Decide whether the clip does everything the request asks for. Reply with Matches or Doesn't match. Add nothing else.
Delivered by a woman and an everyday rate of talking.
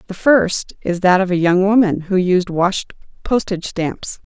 Matches